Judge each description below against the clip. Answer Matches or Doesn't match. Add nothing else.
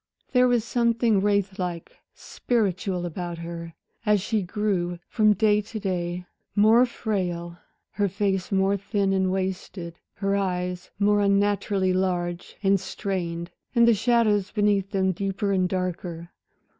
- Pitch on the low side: Doesn't match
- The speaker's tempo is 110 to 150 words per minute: Matches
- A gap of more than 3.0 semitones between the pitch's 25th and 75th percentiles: Doesn't match